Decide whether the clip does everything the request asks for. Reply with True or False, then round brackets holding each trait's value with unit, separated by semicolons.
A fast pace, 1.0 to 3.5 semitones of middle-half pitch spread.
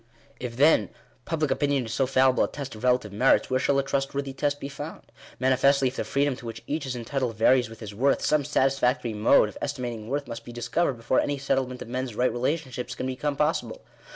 True (215 wpm; 2.6 semitones)